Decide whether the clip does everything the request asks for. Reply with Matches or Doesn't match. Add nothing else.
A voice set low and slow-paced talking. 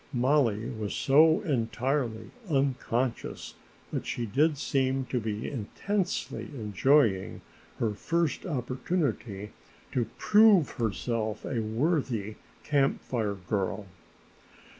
Matches